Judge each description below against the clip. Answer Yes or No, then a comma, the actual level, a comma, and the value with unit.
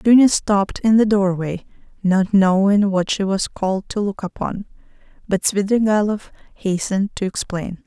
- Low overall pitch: No, high, 200 Hz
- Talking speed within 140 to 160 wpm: Yes, average, 145 wpm